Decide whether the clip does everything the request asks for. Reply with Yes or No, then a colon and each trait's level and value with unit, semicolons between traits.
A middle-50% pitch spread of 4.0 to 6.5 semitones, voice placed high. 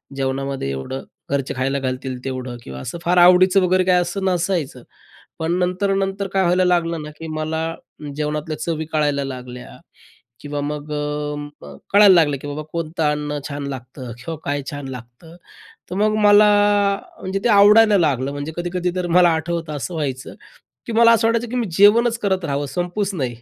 No: average, 4.7 semitones; medium, 160 Hz